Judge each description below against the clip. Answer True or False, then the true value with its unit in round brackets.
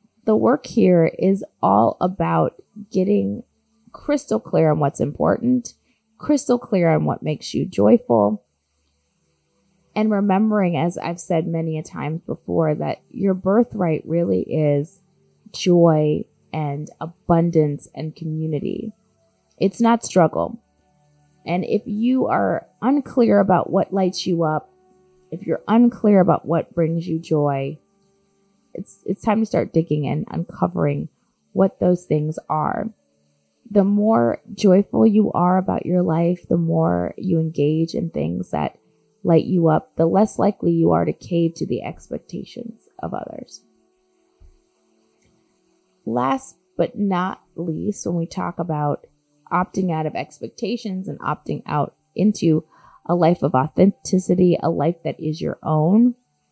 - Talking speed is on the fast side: False (135 wpm)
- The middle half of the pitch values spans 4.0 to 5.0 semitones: True (4.7 semitones)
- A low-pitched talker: False (175 Hz)